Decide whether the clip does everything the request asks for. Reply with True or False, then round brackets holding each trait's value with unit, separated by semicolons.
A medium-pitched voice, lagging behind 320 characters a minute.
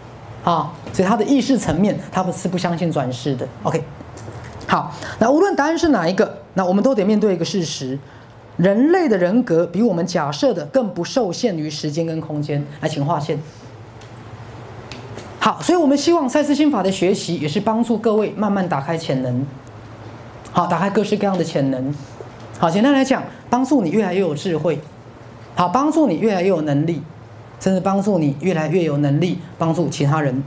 True (170 Hz; 280 characters per minute)